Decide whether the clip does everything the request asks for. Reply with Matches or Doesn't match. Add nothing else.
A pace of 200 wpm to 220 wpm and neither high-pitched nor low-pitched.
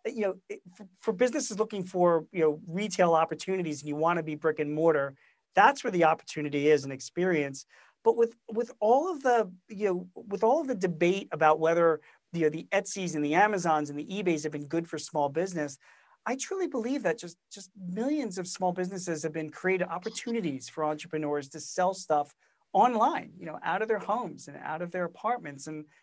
Matches